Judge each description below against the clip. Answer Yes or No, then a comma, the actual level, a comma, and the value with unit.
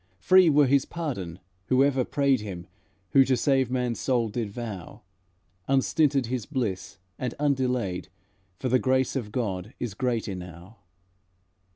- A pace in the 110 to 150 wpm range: Yes, average, 140 wpm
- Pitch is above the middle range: No, low, 125 Hz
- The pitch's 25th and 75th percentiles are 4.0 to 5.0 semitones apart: Yes, average, 4.4 semitones